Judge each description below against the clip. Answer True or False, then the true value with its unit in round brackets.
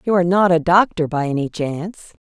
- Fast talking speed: True (210 wpm)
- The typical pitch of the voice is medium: True (170 Hz)